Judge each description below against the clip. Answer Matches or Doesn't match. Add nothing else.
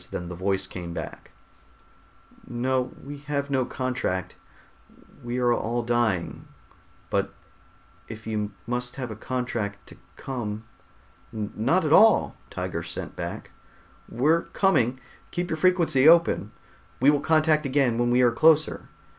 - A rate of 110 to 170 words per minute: Matches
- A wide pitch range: Doesn't match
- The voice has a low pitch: Matches